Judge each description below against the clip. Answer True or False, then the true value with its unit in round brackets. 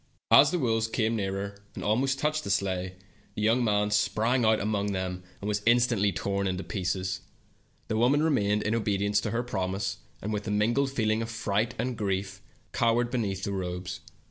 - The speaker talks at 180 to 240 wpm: True (185 wpm)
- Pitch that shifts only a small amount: False (3.0 semitones)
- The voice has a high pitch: False (105 Hz)